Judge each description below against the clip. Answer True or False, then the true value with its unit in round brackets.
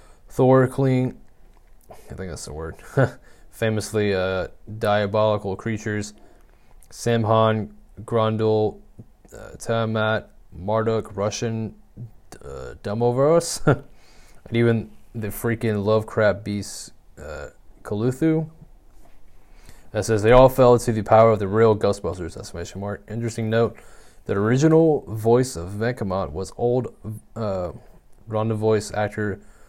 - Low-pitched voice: True (110 Hz)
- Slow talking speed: True (110 wpm)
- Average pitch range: False (2.2 semitones)